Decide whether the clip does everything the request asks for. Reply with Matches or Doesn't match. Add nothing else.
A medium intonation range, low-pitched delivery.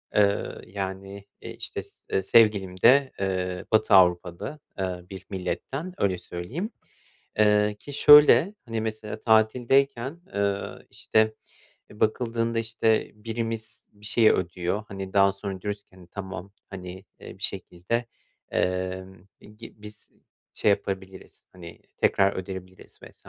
Matches